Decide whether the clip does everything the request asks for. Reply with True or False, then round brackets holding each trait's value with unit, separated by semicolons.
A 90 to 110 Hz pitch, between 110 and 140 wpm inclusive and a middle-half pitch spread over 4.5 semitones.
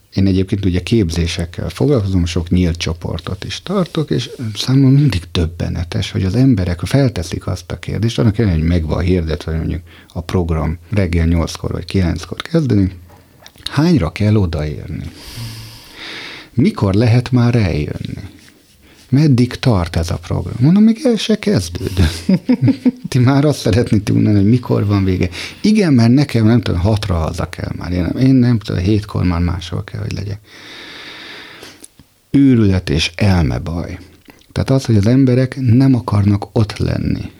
False (100 Hz; 150 wpm; 5.6 semitones)